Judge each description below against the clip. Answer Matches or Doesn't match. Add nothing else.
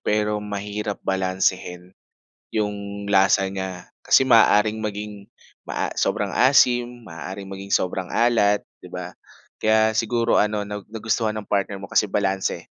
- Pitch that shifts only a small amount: Matches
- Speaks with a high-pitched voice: Doesn't match